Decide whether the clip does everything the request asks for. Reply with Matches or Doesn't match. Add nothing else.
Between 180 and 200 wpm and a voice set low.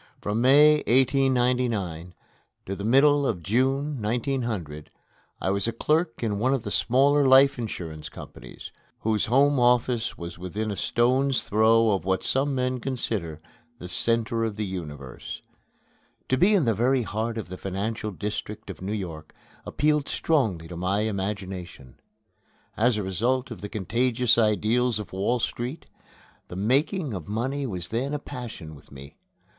Doesn't match